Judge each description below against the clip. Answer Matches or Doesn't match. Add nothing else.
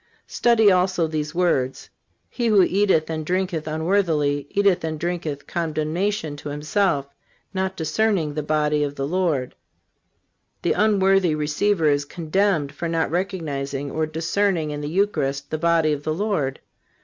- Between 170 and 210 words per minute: Doesn't match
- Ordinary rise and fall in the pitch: Matches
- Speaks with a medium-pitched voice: Matches